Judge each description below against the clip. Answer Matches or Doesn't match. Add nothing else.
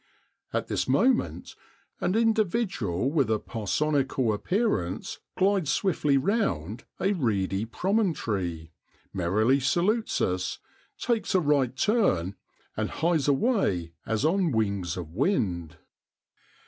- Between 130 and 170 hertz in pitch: Matches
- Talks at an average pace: Doesn't match